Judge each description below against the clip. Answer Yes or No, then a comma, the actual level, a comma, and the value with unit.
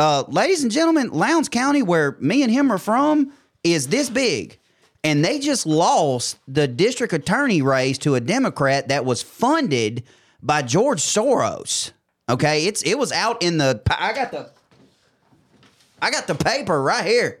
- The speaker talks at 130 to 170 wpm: Yes, average, 165 wpm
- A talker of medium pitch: Yes, medium, 165 Hz